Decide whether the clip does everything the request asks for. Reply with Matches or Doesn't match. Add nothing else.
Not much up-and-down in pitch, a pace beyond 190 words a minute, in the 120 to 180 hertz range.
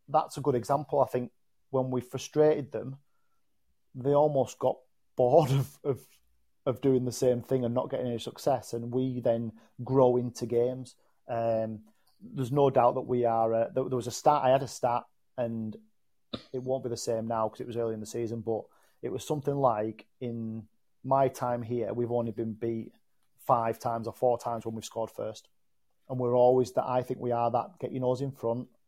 Matches